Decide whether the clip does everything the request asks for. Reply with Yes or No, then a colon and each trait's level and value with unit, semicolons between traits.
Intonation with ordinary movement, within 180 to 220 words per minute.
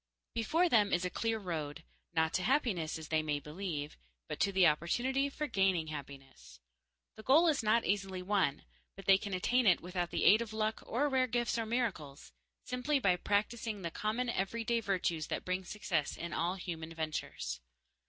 No: wide, 5.9 semitones; average, 185 wpm